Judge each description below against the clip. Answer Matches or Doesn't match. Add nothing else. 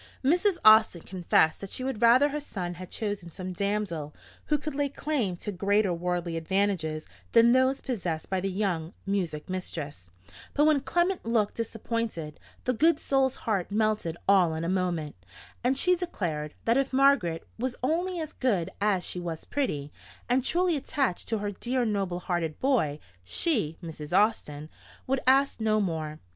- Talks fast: Doesn't match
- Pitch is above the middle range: Matches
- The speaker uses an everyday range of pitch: Doesn't match